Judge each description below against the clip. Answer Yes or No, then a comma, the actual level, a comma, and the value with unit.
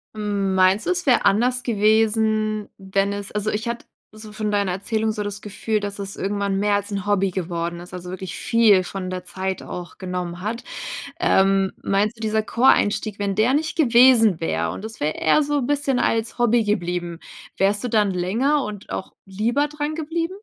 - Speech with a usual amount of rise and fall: Yes, average, 3.1 semitones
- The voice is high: Yes, high, 210 Hz